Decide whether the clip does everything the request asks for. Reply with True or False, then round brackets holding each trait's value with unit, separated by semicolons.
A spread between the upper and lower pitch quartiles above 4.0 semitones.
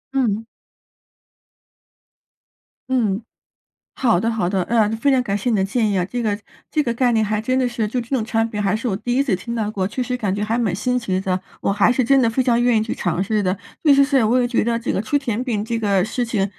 False (3.2 semitones)